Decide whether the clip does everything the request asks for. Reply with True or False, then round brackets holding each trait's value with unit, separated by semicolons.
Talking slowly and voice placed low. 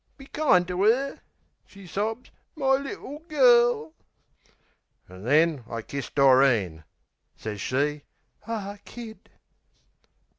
False (105 wpm; 185 Hz)